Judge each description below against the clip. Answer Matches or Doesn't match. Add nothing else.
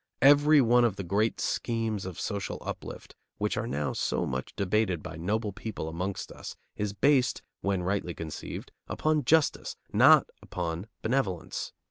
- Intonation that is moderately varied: Matches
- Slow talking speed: Doesn't match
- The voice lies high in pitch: Doesn't match